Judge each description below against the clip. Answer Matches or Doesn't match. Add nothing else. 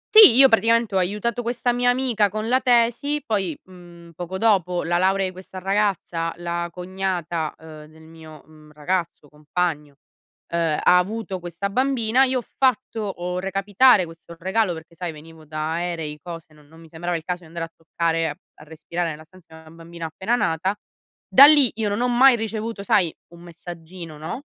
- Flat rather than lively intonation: Doesn't match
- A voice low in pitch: Doesn't match